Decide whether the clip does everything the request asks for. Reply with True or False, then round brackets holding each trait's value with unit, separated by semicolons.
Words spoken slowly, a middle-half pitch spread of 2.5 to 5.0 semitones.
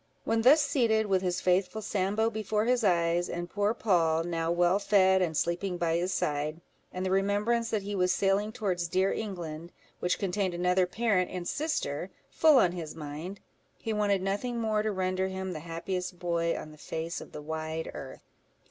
False (185 wpm; 3.4 semitones)